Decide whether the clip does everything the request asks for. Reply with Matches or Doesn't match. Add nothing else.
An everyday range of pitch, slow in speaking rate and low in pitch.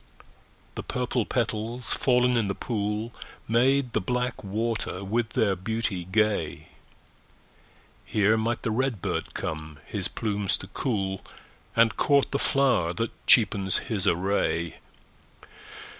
Matches